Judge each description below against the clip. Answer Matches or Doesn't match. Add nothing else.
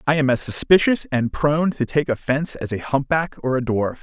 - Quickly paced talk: Matches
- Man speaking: Matches